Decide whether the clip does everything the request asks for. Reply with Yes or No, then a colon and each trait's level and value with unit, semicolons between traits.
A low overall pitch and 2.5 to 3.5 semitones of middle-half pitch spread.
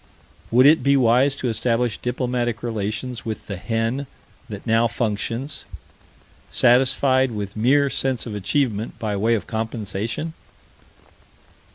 Yes: low, 115 Hz; average, 2.9 semitones